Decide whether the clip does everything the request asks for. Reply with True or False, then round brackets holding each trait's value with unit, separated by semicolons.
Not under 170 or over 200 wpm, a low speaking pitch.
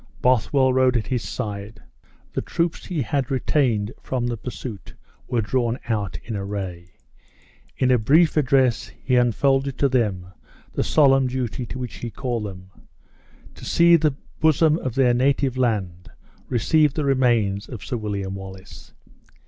False (155 wpm; 125 Hz)